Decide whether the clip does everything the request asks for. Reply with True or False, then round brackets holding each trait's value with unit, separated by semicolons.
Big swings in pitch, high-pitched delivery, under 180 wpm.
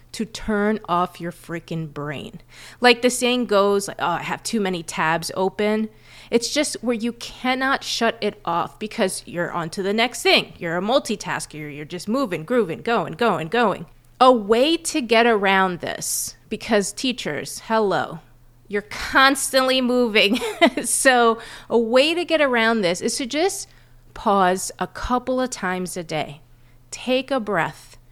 True (6.4 semitones; 210 Hz; 155 wpm)